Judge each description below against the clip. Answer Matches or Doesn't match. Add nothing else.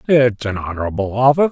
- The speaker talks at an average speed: Matches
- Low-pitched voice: Matches